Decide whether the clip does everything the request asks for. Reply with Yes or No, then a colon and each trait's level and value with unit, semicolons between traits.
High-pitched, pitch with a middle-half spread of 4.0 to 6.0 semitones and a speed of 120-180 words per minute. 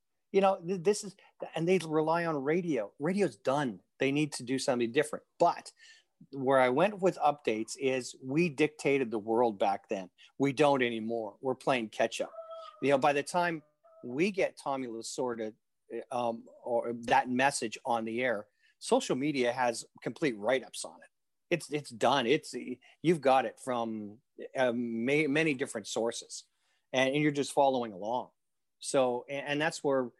No: medium, 140 Hz; average, 4.6 semitones; average, 165 wpm